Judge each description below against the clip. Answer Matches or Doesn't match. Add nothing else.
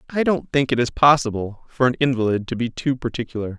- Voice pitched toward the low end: Matches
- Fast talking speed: Matches